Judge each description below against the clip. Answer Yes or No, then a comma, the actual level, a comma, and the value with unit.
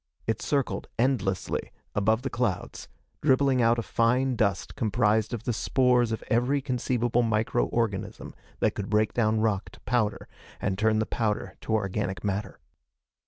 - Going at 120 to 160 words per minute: Yes, average, 150 wpm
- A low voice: Yes, low, 115 Hz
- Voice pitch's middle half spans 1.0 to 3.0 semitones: Yes, average, 2.7 semitones